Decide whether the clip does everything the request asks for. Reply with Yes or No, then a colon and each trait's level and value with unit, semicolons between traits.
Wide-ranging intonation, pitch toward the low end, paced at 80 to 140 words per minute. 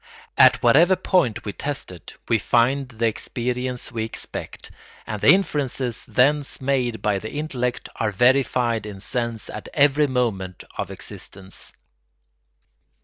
No: average, 3.6 semitones; low, 125 Hz; slow, 135 wpm